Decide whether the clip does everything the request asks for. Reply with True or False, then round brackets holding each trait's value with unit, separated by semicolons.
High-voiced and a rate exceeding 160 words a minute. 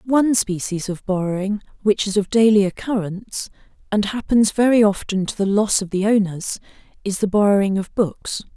True (205 Hz; 170 wpm)